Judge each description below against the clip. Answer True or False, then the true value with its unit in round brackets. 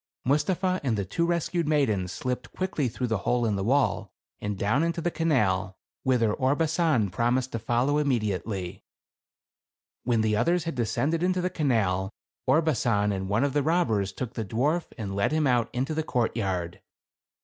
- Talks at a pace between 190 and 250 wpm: False (170 wpm)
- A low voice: True (125 Hz)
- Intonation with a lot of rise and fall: True (6.8 semitones)